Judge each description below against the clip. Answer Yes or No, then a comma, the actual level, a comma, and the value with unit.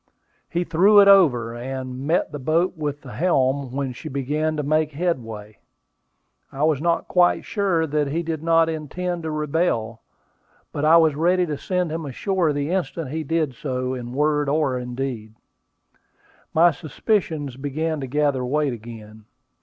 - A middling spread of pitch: Yes, average, 4.0 semitones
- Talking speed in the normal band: Yes, average, 160 wpm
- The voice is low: No, medium, 150 Hz